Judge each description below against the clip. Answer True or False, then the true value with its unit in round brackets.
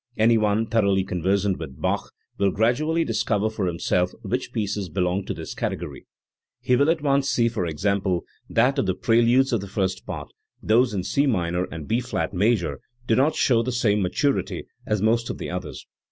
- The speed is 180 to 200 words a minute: True (190 wpm)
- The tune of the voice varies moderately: True (4.3 semitones)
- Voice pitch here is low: True (105 Hz)